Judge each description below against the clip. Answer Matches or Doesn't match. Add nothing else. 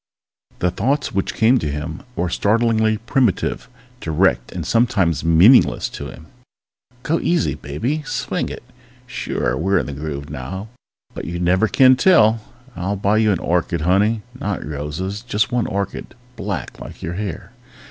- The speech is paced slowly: Doesn't match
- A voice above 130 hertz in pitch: Doesn't match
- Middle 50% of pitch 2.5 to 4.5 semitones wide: Doesn't match